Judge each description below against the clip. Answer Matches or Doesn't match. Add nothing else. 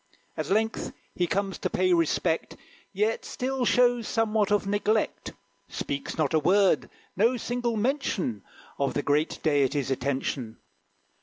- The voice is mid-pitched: Doesn't match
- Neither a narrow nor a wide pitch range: Doesn't match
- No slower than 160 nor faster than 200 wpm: Doesn't match